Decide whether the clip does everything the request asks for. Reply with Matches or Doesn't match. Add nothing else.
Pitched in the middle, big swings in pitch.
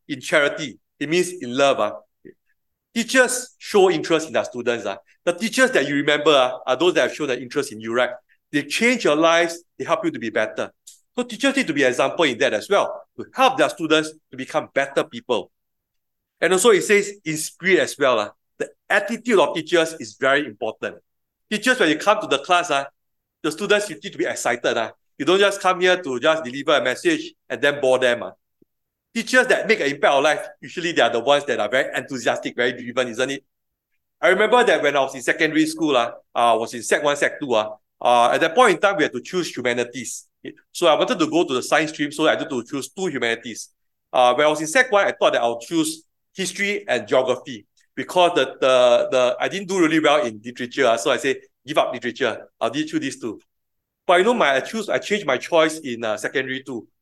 Matches